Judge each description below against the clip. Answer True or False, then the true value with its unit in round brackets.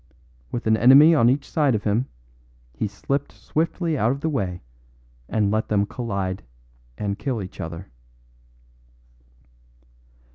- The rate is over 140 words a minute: False (135 wpm)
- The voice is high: False (115 Hz)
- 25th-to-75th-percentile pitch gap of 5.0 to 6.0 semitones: True (5.6 semitones)